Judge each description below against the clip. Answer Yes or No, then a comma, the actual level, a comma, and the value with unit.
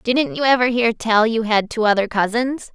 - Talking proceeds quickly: Yes, fast, 220 wpm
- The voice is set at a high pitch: Yes, high, 230 Hz